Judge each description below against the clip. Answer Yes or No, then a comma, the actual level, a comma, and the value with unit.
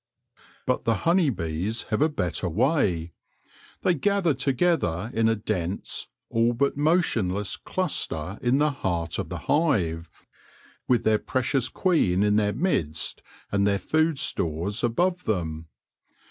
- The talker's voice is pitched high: No, low, 110 Hz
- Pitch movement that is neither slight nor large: No, wide, 8.5 semitones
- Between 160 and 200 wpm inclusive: No, slow, 135 wpm